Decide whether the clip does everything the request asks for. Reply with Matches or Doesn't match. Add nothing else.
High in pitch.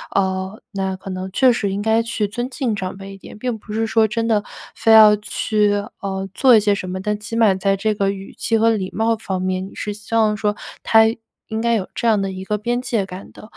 Matches